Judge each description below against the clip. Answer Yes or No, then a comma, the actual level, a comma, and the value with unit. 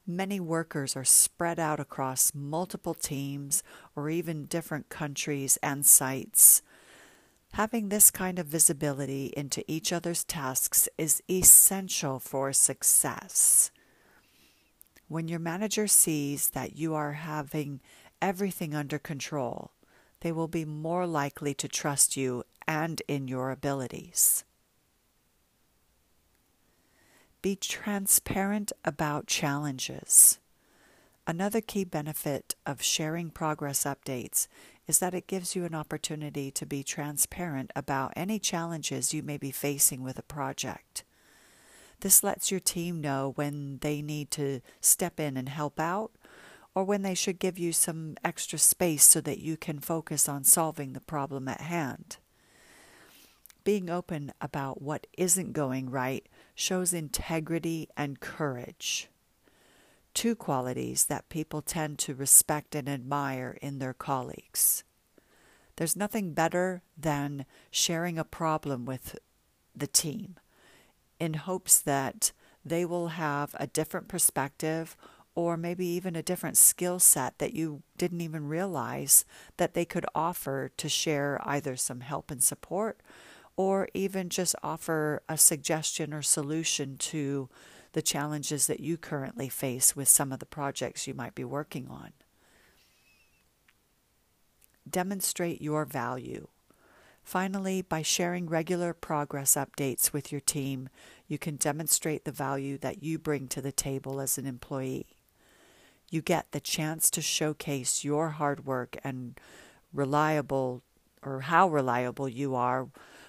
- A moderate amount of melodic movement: Yes, average, 3.5 semitones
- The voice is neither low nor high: Yes, medium, 150 Hz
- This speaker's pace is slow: Yes, slow, 130 wpm